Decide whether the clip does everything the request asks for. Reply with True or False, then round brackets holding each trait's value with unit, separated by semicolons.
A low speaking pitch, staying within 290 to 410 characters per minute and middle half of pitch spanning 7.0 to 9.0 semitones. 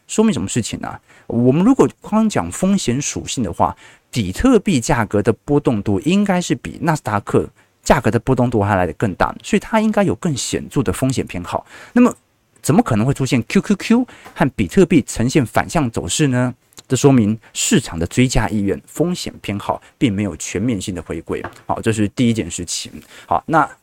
True (125 Hz; 295 characters per minute; 8.5 semitones)